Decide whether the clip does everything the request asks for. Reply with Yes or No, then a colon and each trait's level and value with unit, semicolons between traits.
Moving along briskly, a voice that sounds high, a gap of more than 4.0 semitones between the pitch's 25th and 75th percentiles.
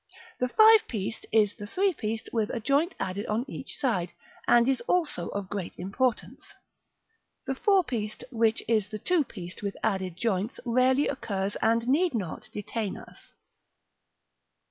No: average, 155 wpm; high, 225 Hz; average, 4.5 semitones